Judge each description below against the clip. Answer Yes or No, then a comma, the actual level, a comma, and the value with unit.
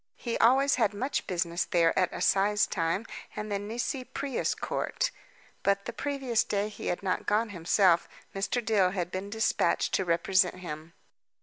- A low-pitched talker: No, high, 200 Hz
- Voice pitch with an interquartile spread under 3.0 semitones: No, average, 4.0 semitones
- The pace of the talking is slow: No, average, 165 wpm